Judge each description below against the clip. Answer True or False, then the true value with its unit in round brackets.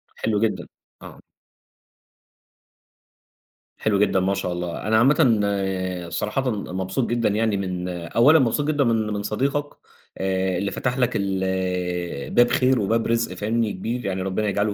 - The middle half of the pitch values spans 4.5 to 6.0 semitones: False (3.9 semitones)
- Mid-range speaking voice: False (105 Hz)